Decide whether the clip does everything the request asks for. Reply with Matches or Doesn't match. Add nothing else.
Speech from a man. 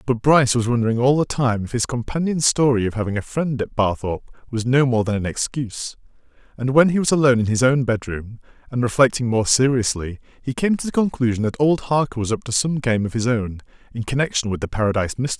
Matches